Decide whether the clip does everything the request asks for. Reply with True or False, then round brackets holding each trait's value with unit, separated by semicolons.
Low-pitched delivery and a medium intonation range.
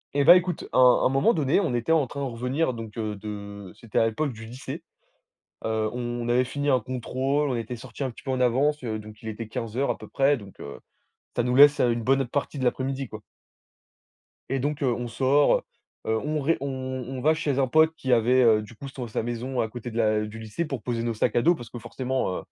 True (125 Hz; 3.4 semitones)